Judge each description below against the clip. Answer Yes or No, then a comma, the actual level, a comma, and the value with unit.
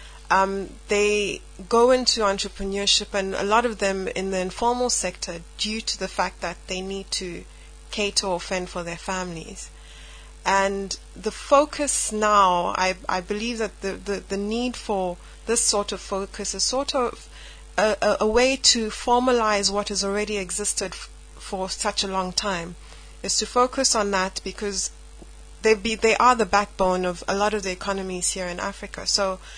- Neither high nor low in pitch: No, high, 200 Hz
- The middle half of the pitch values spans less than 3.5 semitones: Yes, narrow, 2.5 semitones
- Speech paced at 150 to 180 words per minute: Yes, average, 175 wpm